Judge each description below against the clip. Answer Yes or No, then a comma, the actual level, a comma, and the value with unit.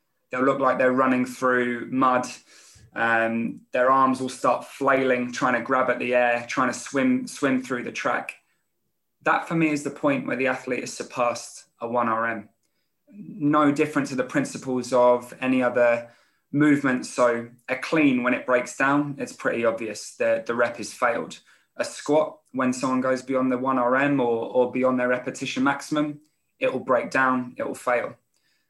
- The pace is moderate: Yes, average, 175 wpm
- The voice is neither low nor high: No, low, 130 Hz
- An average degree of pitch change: No, narrow, 1.9 semitones